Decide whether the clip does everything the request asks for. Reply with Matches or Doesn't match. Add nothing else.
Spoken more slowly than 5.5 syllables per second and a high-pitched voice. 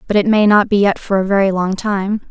Doesn't match